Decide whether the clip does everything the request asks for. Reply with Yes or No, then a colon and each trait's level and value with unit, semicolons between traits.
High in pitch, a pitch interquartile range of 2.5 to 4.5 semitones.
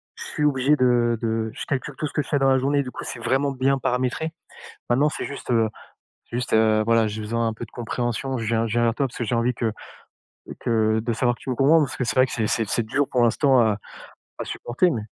No: low, 120 Hz; average, 2.9 semitones